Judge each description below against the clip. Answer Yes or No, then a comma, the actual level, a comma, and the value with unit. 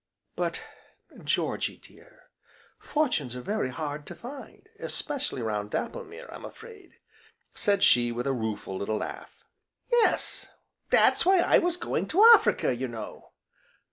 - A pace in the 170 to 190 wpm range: No, slow, 135 wpm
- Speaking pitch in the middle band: Yes, medium, 170 Hz